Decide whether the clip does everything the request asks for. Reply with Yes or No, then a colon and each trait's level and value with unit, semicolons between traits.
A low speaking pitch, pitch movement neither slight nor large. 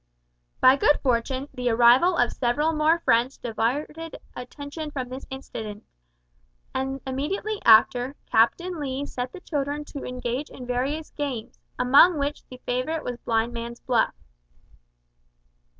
No: very high, 265 Hz; average, 3.3 semitones